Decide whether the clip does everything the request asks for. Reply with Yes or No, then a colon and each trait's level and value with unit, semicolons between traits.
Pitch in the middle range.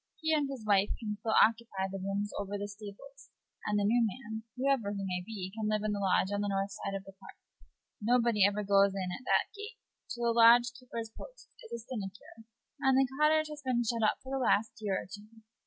No: high, 215 Hz